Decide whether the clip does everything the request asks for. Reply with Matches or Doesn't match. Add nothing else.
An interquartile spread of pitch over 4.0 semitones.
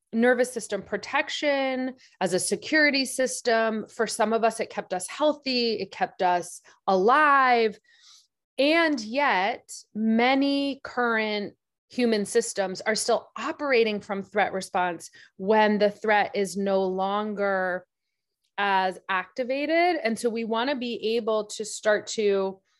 Matches